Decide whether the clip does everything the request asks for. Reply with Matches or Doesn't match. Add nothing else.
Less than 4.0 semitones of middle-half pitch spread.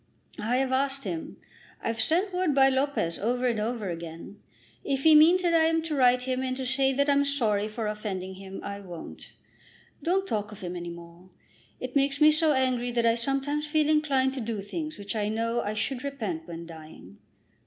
Doesn't match